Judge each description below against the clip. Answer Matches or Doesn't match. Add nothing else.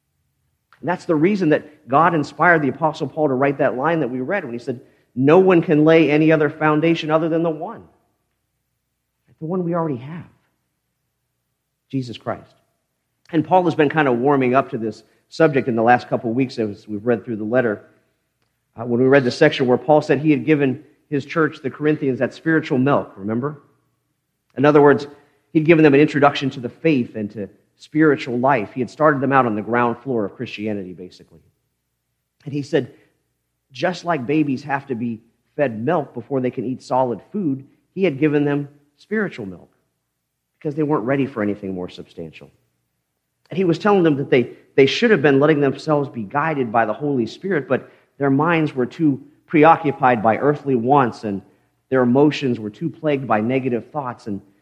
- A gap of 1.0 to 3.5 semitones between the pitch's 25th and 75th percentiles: Doesn't match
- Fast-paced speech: Doesn't match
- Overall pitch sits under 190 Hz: Matches